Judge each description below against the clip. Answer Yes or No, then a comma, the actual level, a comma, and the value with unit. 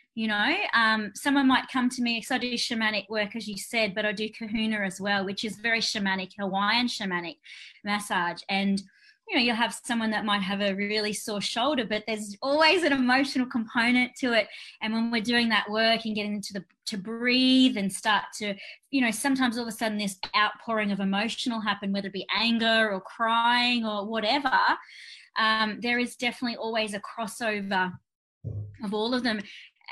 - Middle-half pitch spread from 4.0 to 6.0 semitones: No, average, 2.9 semitones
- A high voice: Yes, high, 220 Hz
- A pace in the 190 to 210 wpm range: Yes, average, 195 wpm